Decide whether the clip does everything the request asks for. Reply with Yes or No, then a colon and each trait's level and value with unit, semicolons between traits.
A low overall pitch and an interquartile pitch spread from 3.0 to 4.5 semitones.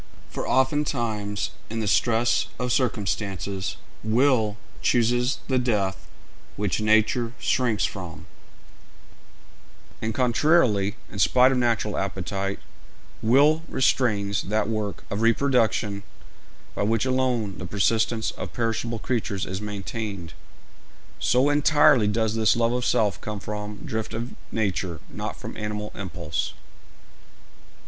Yes: low, 110 Hz; average, 3.3 semitones